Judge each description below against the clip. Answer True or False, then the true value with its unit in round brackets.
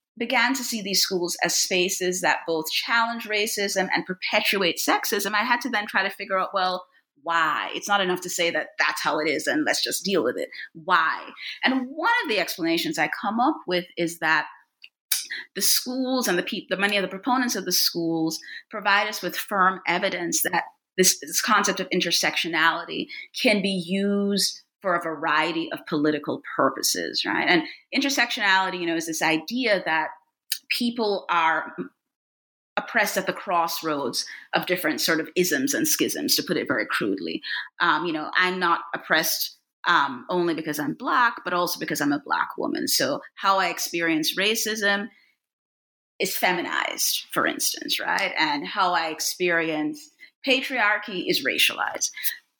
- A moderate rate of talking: True (165 wpm)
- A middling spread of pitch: False (5.9 semitones)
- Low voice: False (190 Hz)